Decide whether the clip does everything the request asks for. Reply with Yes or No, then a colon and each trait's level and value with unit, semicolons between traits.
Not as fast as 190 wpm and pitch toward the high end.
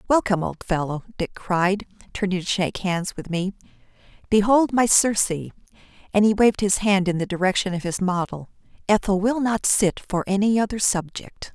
Yes: average, 170 wpm; high, 195 Hz